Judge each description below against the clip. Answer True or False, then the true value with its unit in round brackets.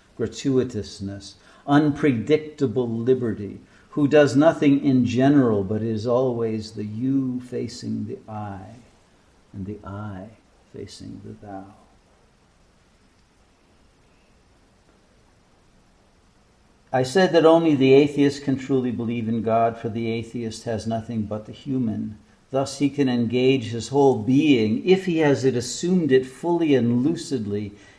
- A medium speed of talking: False (120 wpm)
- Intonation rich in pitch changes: False (4.2 semitones)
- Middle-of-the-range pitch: False (120 Hz)